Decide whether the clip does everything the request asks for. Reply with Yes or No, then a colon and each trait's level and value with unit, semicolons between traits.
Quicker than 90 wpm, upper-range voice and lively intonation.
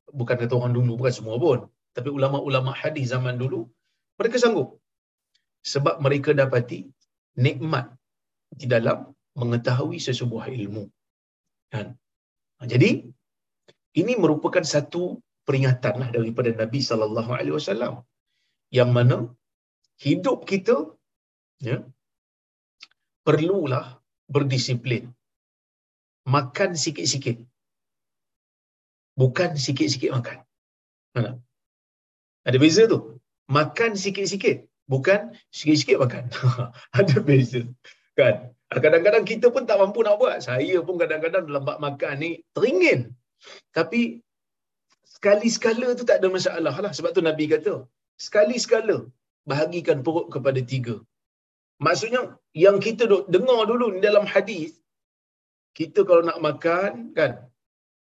No: average, 105 wpm; medium, 140 Hz; wide, 6.6 semitones